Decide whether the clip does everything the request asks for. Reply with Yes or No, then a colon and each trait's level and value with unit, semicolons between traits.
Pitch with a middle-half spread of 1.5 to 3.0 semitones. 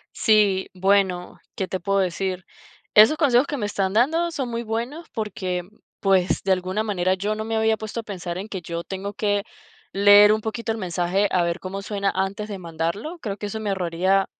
Yes: average, 2.7 semitones